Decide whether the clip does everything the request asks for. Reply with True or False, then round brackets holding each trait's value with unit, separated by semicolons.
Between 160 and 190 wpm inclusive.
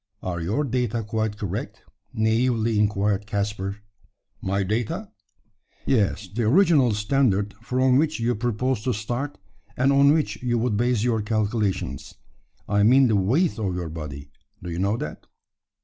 False (150 wpm)